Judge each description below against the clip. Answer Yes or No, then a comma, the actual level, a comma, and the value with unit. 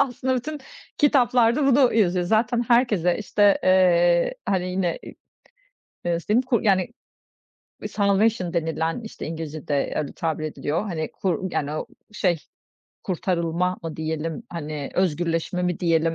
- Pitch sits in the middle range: Yes, medium, 180 Hz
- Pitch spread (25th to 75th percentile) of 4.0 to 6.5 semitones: Yes, average, 4.9 semitones